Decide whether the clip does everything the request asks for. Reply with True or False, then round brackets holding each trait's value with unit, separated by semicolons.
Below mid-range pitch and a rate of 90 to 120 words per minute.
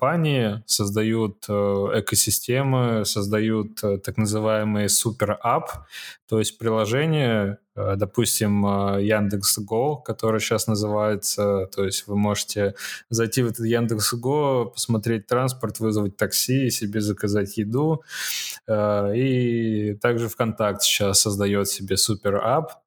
True (110 Hz; 110 wpm)